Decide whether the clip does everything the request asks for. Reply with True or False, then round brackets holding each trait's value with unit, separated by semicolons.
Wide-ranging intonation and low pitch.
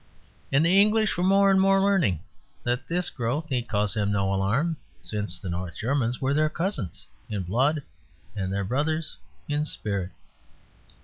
True (8.6 semitones; 130 Hz)